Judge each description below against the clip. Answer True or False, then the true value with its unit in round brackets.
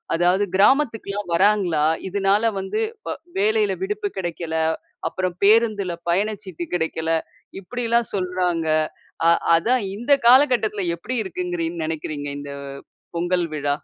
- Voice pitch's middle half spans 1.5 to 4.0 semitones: False (4.7 semitones)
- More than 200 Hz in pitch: False (190 Hz)